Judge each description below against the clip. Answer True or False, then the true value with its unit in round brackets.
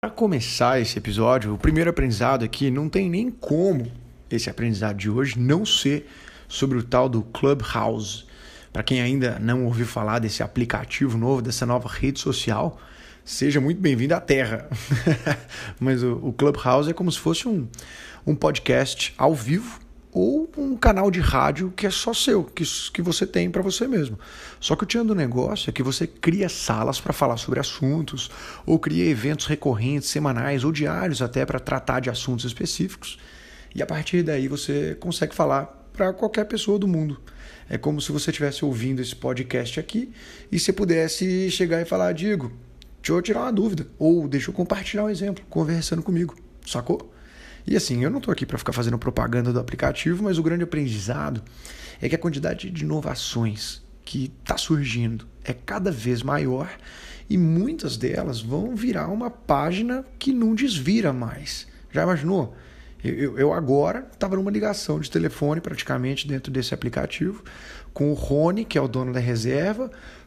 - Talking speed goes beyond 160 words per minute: True (170 wpm)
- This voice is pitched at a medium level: True (145 Hz)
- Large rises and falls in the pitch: True (6.7 semitones)